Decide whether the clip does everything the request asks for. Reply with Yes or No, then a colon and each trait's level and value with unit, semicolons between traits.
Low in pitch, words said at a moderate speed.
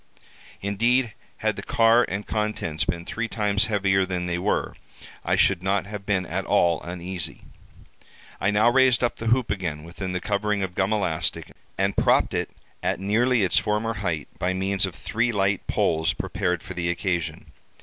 Yes: low, 100 Hz; average, 175 wpm